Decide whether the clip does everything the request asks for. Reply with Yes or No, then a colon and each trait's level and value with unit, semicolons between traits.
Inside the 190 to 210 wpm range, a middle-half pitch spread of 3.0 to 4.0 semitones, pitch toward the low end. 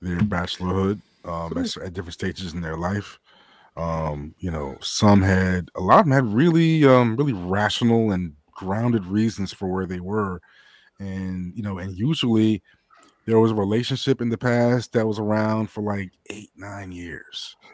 No: average, 175 wpm; average, 3.7 semitones; low, 100 Hz